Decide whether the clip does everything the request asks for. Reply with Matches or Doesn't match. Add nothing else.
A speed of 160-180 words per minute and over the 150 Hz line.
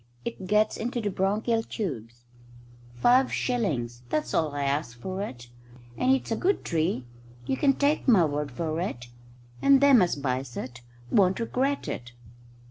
Matches